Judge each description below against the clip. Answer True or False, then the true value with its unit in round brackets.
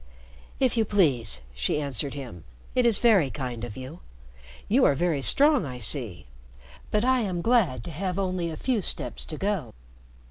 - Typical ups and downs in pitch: False (8.4 semitones)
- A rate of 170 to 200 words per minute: True (175 wpm)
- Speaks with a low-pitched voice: False (165 Hz)